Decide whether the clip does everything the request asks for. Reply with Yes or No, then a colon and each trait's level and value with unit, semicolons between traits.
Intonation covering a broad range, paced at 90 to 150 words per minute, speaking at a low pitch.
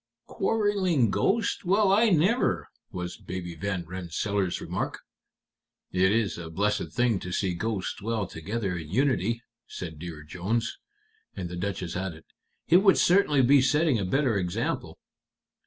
Yes: wide, 7.9 semitones; average, 140 wpm; low, 100 Hz